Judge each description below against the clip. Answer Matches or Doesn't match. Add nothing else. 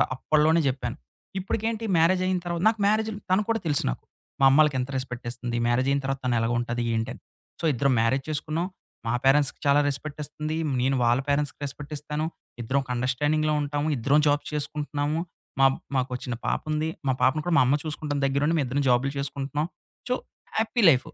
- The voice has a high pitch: Doesn't match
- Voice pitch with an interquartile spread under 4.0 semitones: Matches